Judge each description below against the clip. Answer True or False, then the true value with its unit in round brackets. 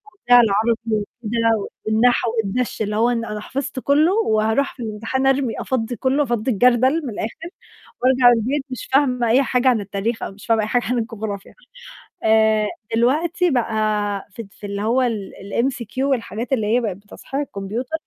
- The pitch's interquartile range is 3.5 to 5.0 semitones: False (3.1 semitones)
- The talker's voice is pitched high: True (235 Hz)